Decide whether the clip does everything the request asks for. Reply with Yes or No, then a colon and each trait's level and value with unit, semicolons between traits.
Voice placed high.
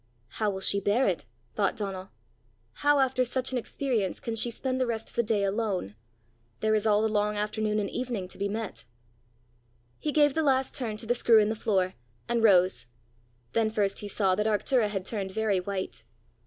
Yes: high, 215 Hz